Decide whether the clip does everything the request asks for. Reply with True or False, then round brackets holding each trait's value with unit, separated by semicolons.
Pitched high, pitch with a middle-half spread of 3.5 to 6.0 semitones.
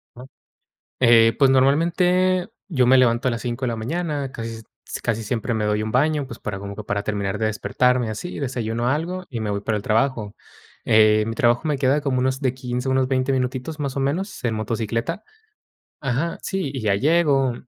False (125 Hz; 3.9 semitones)